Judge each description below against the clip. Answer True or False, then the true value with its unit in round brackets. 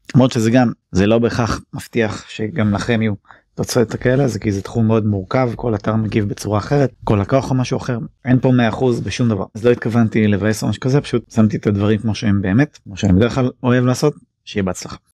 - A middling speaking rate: False (215 wpm)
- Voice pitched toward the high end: False (115 Hz)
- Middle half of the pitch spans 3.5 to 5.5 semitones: False (2.9 semitones)